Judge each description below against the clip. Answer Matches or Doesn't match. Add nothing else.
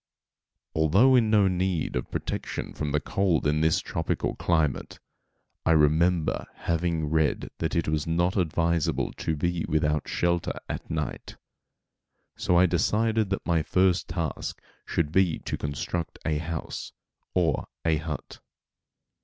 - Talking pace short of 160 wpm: Matches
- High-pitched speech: Doesn't match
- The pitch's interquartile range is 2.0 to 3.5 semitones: Matches